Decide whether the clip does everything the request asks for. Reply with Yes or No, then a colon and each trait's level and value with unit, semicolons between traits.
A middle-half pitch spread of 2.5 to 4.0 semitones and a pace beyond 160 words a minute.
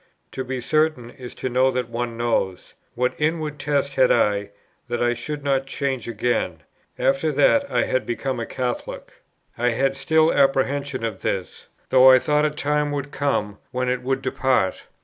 Yes: average, 2.9 semitones; average, 175 wpm